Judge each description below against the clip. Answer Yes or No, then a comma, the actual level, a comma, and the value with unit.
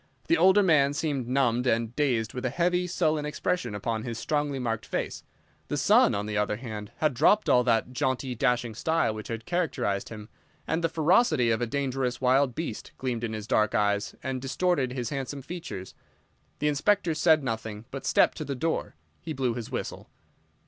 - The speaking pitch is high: No, low, 130 Hz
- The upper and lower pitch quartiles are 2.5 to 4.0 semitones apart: No, average, 5.2 semitones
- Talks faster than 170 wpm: Yes, average, 190 wpm